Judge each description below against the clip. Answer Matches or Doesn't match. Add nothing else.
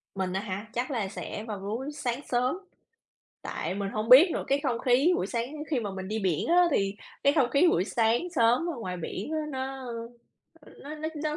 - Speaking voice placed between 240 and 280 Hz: Matches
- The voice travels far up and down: Matches